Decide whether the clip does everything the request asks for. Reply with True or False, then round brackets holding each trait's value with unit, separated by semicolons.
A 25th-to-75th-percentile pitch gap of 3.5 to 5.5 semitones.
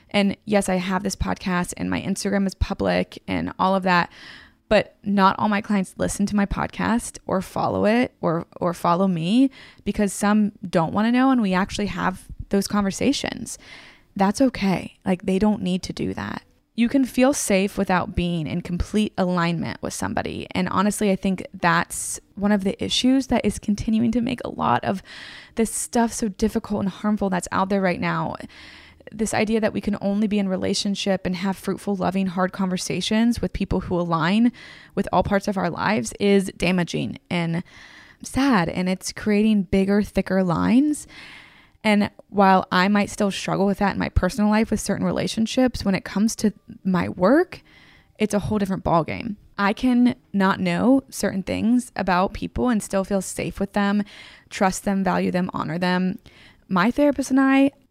False (2.7 semitones)